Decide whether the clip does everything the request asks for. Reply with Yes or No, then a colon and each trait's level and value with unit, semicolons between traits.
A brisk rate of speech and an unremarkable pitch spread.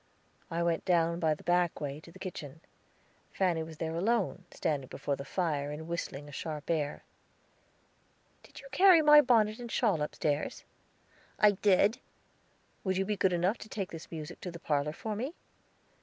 No: average, 175 wpm; average, 5.0 semitones